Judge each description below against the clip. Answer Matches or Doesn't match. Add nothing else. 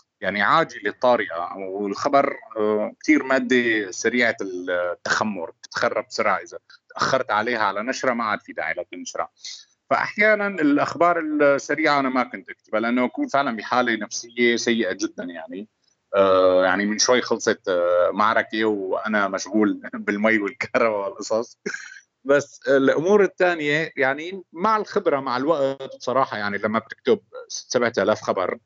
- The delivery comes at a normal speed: Doesn't match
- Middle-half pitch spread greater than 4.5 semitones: Matches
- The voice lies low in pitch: Matches